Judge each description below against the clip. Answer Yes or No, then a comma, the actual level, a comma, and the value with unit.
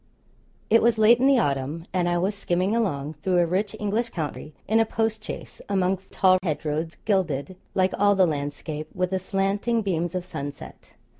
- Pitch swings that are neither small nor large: Yes, average, 4.4 semitones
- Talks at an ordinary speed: Yes, average, 175 wpm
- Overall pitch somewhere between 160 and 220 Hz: Yes, medium, 185 Hz